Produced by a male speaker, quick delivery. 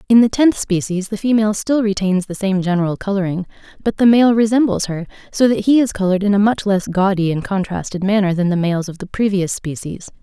No: female; fast, 215 wpm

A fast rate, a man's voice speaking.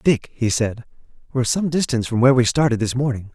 Yes: fast, 215 wpm; male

